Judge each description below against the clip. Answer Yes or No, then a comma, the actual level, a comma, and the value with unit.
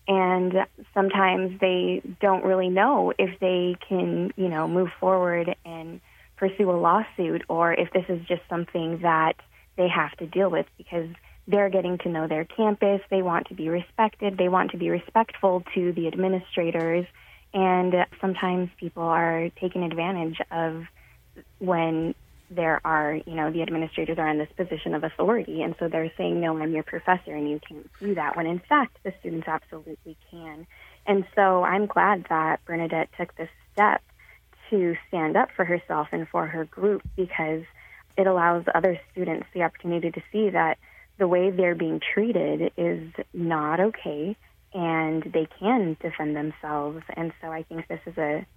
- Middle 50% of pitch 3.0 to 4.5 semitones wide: No, narrow, 2.5 semitones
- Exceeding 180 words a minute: No, average, 170 wpm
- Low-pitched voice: No, medium, 175 Hz